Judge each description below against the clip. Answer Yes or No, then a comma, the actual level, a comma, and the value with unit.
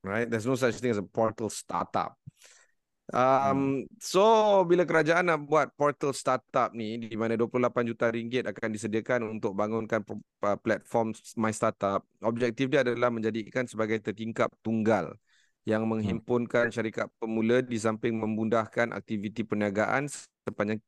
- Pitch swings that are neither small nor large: No, narrow, 2.3 semitones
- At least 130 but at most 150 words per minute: Yes, average, 135 wpm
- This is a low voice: Yes, low, 115 Hz